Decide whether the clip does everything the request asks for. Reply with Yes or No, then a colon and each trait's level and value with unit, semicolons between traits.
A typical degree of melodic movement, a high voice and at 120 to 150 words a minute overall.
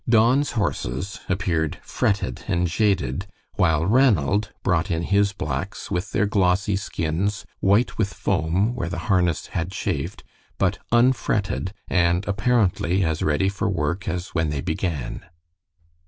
No: average, 3.6 semitones; very low, 95 Hz; slow, 135 wpm